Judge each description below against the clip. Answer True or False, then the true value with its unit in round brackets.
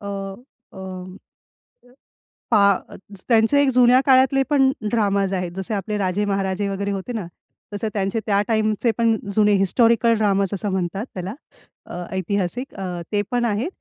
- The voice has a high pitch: True (210 Hz)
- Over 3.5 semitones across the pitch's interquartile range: False (3.2 semitones)